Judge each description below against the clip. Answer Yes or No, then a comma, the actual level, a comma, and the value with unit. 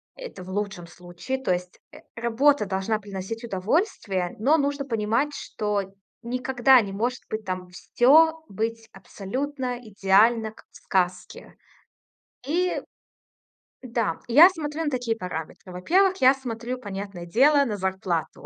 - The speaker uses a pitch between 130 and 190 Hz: No, high, 225 Hz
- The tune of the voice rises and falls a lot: Yes, wide, 5.7 semitones